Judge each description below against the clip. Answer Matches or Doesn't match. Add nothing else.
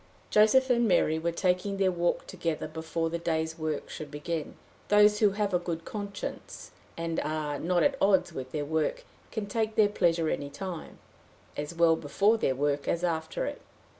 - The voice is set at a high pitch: Doesn't match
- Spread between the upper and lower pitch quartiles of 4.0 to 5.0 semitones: Matches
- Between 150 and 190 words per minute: Matches